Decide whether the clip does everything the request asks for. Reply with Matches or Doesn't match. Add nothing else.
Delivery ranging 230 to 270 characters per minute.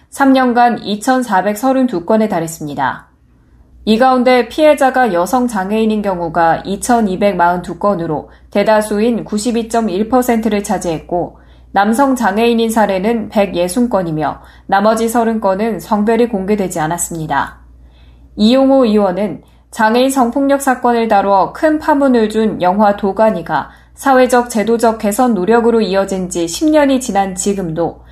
Matches